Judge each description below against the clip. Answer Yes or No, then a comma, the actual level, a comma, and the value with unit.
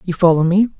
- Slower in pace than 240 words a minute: Yes, fast, 225 wpm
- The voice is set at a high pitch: No, medium, 180 Hz